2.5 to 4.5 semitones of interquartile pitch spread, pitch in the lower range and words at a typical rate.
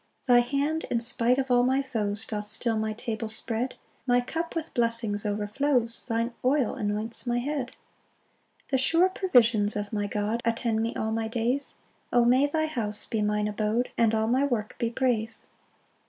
No: average, 2.9 semitones; high, 230 Hz; average, 185 wpm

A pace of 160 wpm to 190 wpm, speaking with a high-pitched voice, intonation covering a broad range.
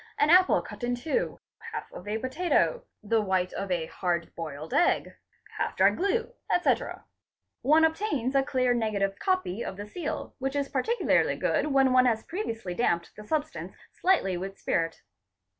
Yes: average, 165 wpm; very high, 250 Hz; wide, 8.5 semitones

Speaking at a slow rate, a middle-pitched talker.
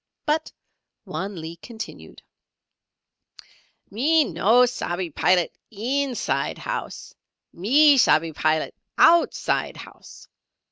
No: slow, 85 wpm; high, 220 Hz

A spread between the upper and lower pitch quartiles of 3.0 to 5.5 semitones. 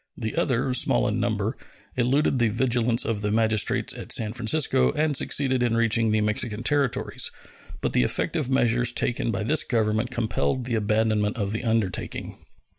No: narrow, 2.6 semitones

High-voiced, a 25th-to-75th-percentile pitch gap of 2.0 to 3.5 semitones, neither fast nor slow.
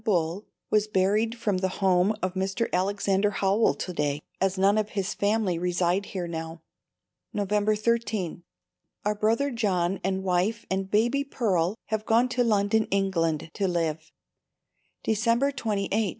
Yes: high, 200 Hz; average, 3.1 semitones; average, 145 wpm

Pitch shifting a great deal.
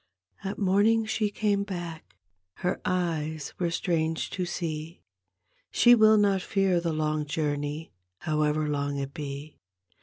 No: average, 4.3 semitones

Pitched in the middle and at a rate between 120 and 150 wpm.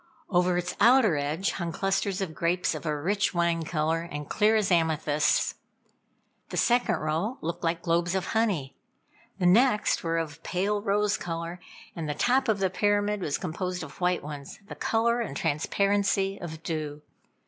No: medium, 180 Hz; average, 170 wpm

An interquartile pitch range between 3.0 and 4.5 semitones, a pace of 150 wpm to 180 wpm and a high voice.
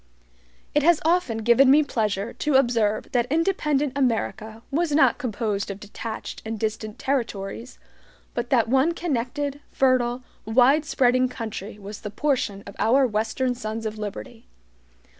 No: average, 3.9 semitones; average, 140 wpm; high, 240 Hz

